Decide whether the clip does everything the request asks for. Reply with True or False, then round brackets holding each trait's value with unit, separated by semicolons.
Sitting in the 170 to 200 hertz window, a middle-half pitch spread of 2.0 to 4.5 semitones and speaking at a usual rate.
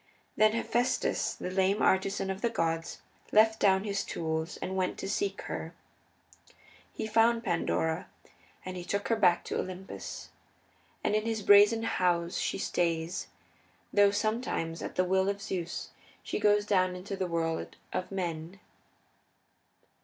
True (190 Hz; 3.1 semitones; 145 wpm)